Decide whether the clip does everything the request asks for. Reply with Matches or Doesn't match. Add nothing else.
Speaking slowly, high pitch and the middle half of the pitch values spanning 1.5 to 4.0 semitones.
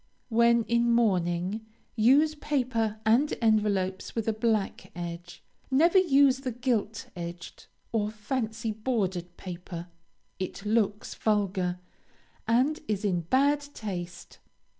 Doesn't match